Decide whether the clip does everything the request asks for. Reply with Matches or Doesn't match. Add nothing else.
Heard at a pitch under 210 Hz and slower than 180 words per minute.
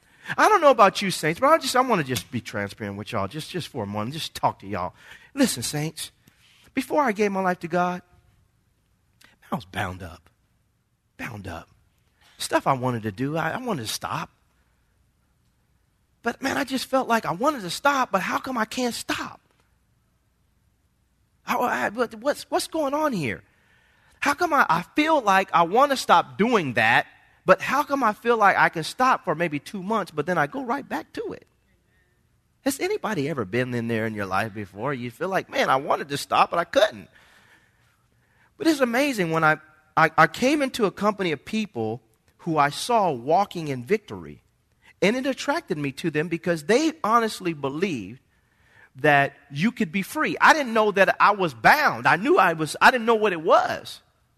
Doesn't match